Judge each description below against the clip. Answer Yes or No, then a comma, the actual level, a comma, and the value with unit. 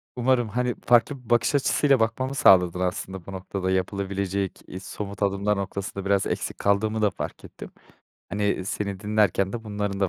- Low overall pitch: Yes, low, 100 Hz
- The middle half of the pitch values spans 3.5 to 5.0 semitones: No, narrow, 2.6 semitones